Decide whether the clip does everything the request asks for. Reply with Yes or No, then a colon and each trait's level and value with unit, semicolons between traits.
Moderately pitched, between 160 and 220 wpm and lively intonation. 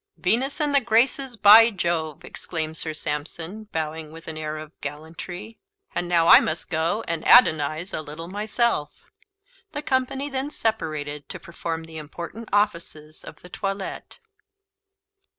No: medium, 170 Hz; average, 145 wpm; wide, 5.9 semitones